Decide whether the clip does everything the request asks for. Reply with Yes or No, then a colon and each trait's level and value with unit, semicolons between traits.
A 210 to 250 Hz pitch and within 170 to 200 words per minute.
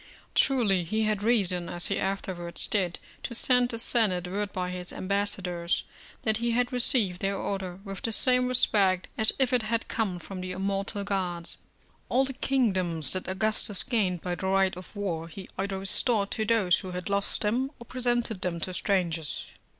No: high, 195 Hz; average, 180 wpm